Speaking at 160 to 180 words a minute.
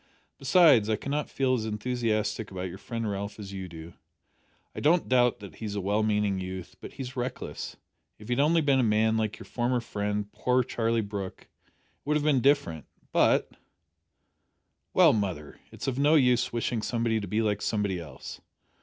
No: average, 195 wpm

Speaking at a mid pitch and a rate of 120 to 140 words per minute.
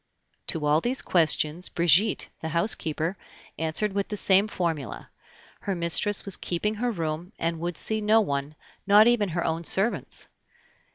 No: medium, 175 Hz; average, 155 wpm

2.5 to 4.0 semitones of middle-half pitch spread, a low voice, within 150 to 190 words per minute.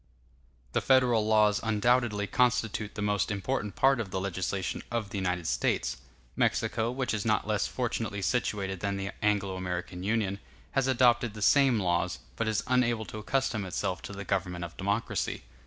Yes: average, 3.4 semitones; low, 105 Hz; average, 170 wpm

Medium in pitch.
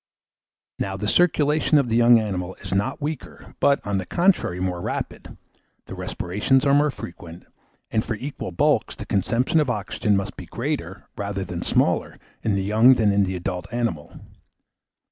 No: low, 105 Hz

